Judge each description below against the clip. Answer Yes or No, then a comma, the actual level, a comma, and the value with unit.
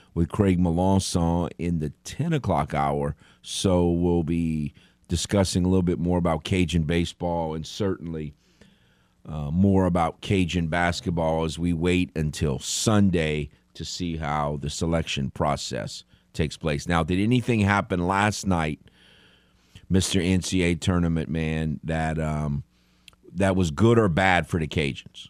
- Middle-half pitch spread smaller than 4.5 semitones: Yes, average, 3.1 semitones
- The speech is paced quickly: No, average, 140 wpm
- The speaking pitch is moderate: No, very low, 85 Hz